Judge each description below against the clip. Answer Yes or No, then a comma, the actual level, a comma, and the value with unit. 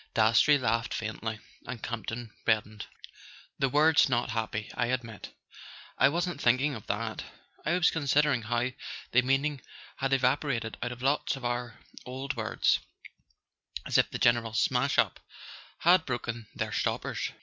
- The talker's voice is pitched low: Yes, low, 125 Hz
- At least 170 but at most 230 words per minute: No, average, 145 wpm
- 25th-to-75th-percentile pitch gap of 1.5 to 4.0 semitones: Yes, average, 3.3 semitones